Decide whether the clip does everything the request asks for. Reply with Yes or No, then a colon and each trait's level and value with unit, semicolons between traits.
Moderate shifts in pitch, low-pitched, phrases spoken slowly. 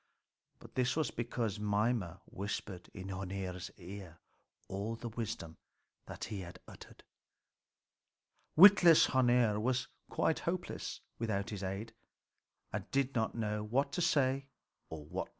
Yes: average, 4.7 semitones; low, 110 Hz; slow, 125 wpm